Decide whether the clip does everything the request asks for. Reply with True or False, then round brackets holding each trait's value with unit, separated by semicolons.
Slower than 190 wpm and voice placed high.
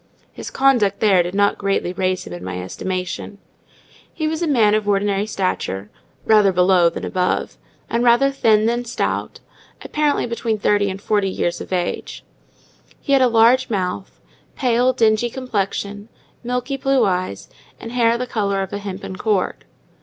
True (155 wpm; 205 Hz)